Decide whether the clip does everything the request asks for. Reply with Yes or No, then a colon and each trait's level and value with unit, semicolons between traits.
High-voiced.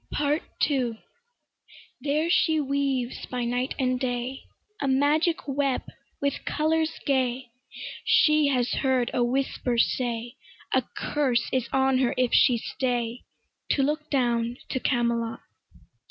Yes: very high, 260 Hz